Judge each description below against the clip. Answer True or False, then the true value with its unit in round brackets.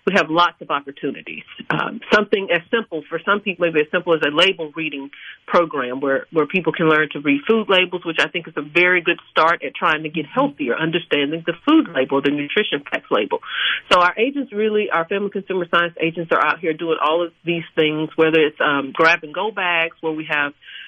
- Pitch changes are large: False (4.2 semitones)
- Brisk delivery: True (220 wpm)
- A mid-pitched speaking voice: True (170 Hz)